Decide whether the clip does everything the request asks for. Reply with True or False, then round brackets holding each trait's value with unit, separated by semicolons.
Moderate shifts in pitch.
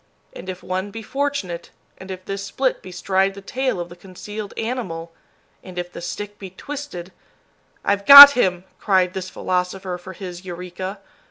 False (2.3 semitones)